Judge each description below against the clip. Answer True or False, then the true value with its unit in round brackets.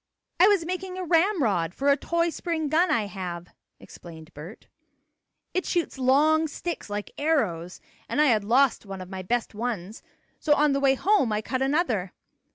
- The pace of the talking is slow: False (175 wpm)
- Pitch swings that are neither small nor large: False (8.3 semitones)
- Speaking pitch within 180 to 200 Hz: False (270 Hz)